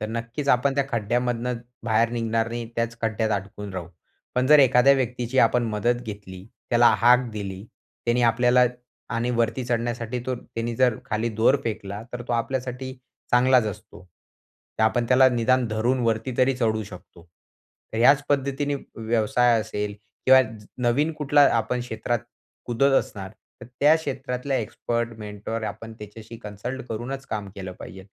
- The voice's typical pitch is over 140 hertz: No, low, 120 Hz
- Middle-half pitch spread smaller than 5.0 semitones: Yes, narrow, 2.5 semitones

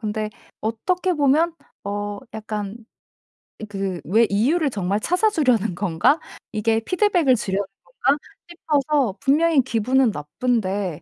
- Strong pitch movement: Yes, wide, 6.4 semitones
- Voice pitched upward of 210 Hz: Yes, high, 225 Hz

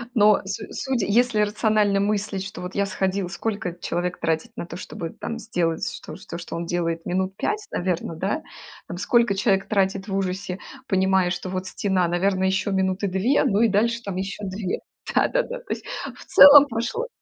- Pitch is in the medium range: No, high, 195 Hz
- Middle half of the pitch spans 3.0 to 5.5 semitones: No, narrow, 2.6 semitones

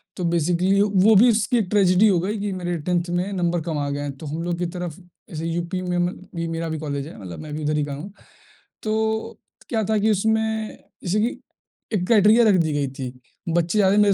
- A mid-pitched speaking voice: Yes, medium, 180 Hz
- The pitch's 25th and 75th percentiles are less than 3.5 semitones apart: No, average, 4.2 semitones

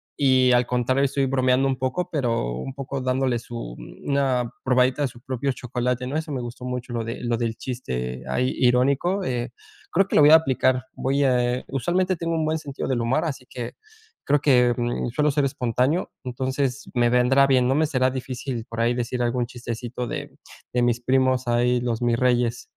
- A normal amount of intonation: No, narrow, 2.0 semitones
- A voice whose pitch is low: Yes, low, 125 Hz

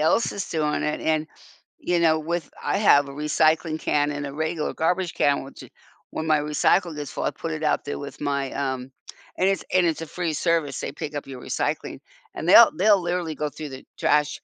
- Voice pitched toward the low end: No, medium, 155 Hz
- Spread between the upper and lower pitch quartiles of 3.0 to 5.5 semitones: No, narrow, 2.6 semitones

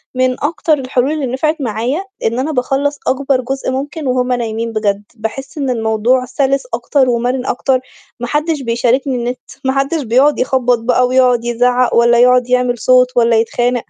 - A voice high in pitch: Yes, very high, 250 Hz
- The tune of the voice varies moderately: No, narrow, 2.1 semitones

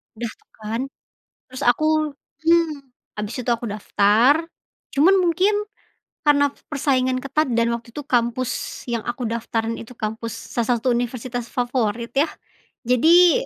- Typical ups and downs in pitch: Yes, average, 3.9 semitones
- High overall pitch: Yes, high, 245 Hz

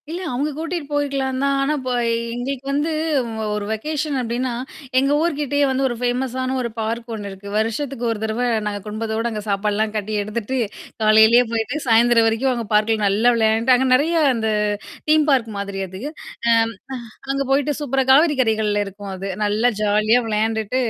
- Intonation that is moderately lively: Yes, average, 3.8 semitones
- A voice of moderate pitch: No, high, 235 Hz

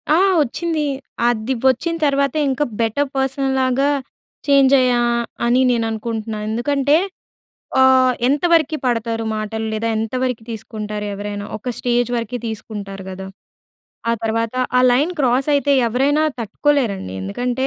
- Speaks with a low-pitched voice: No, high, 245 Hz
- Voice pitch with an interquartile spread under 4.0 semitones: Yes, average, 3.6 semitones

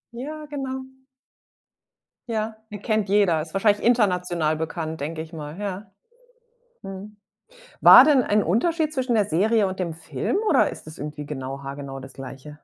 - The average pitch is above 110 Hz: Yes, high, 190 Hz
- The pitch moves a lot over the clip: Yes, wide, 6.2 semitones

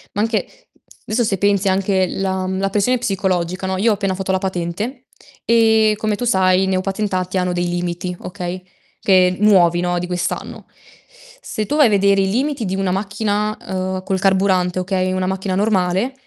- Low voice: No, high, 190 Hz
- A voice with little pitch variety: Yes, narrow, 2.0 semitones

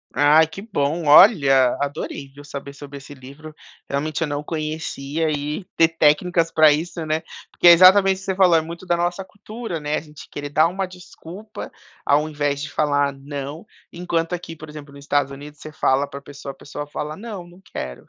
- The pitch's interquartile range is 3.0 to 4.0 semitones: Yes, average, 3.3 semitones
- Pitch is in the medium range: Yes, medium, 155 Hz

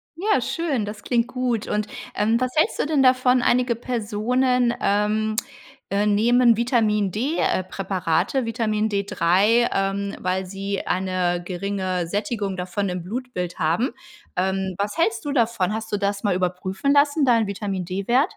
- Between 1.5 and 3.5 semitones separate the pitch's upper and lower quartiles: No, average, 4.3 semitones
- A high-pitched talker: Yes, high, 210 Hz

